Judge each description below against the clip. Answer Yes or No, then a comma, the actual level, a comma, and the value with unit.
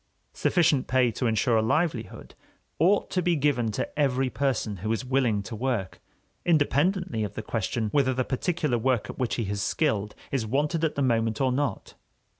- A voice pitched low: Yes, low, 130 Hz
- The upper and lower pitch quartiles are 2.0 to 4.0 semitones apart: No, average, 4.6 semitones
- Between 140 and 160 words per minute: No, average, 185 wpm